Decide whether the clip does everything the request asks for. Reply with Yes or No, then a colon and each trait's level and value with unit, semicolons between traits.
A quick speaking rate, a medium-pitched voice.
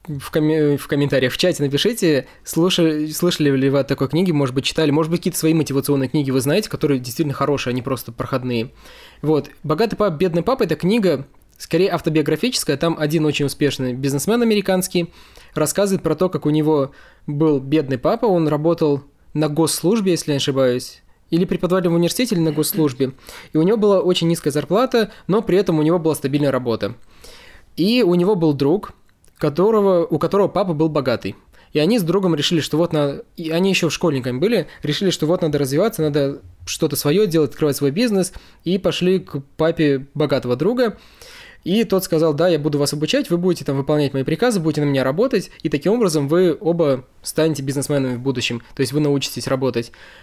Yes: fast, 190 wpm; medium, 155 Hz